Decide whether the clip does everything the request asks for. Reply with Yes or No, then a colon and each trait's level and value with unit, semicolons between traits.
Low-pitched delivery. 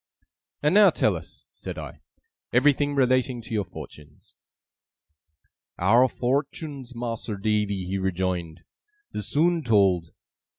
Yes: low, 115 Hz